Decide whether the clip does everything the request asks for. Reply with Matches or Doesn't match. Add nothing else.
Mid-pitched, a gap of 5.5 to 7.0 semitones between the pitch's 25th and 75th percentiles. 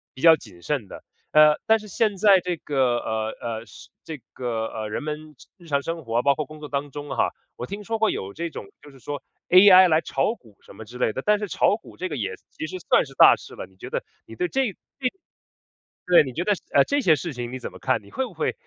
Matches